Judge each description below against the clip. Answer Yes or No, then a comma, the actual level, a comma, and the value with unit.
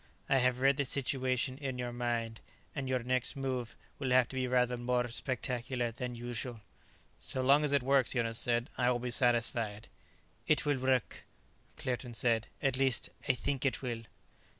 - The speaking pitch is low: Yes, low, 125 Hz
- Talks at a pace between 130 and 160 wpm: No, average, 175 wpm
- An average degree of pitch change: No, narrow, 1.6 semitones